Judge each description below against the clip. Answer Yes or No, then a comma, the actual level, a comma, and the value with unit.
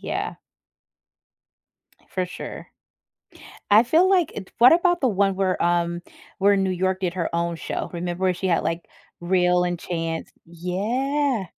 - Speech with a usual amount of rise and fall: Yes, average, 3.6 semitones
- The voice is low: No, medium, 185 Hz